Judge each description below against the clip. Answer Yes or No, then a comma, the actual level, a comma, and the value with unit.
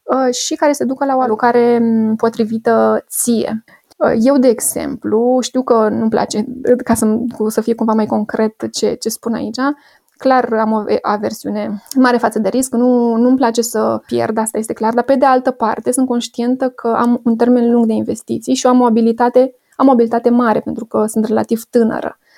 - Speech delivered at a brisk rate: Yes, fast, 185 wpm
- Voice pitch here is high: Yes, high, 235 Hz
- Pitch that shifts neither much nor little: No, narrow, 2.1 semitones